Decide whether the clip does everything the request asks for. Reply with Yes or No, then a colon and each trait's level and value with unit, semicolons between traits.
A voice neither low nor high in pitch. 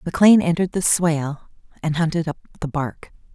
Yes: medium, 160 Hz